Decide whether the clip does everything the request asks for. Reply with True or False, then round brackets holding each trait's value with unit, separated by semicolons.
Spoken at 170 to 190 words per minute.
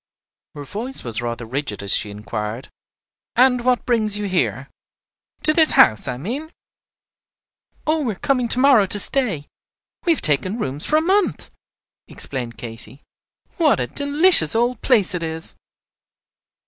False (155 wpm)